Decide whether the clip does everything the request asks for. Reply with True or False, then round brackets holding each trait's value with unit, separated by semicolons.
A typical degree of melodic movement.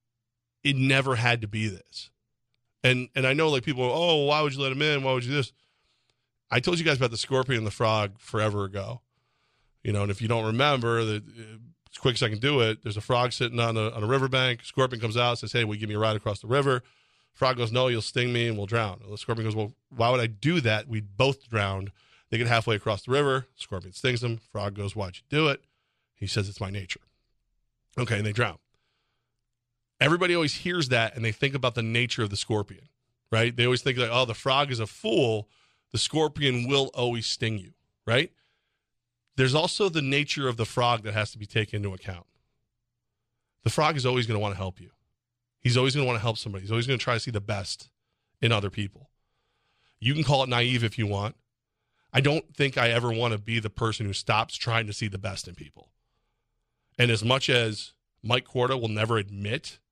True (3.0 semitones)